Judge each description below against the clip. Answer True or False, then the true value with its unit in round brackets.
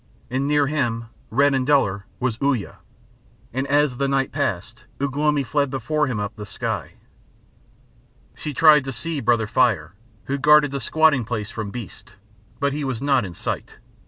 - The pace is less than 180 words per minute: True (170 wpm)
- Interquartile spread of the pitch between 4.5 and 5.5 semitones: False (4.0 semitones)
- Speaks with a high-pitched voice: False (135 Hz)